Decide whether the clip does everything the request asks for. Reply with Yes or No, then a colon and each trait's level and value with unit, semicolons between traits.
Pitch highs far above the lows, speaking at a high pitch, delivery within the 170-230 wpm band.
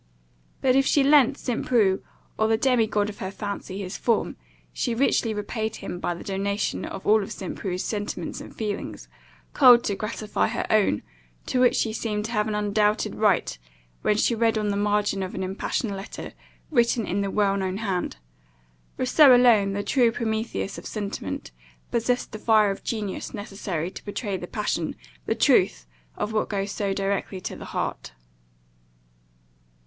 No: narrow, 2.5 semitones; high, 210 Hz; average, 175 wpm